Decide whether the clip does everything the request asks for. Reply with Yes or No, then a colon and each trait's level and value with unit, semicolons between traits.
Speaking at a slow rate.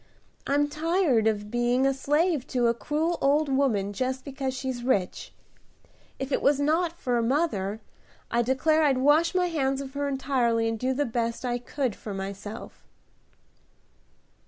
No: average, 160 wpm